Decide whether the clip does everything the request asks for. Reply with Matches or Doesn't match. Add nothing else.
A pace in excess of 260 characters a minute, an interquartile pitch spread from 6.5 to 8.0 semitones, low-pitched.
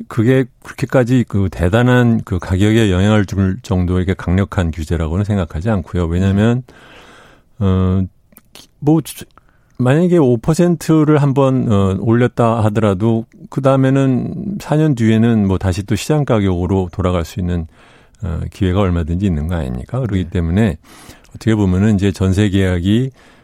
Doesn't match